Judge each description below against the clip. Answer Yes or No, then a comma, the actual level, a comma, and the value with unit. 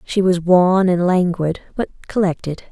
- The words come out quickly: No, average, 155 wpm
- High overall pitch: No, medium, 180 Hz